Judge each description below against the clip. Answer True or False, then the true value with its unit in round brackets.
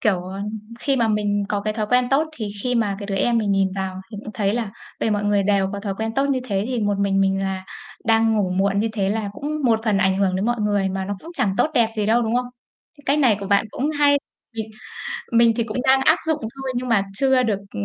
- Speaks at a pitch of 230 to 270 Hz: False (215 Hz)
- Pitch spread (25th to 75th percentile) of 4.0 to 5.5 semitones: False (3.4 semitones)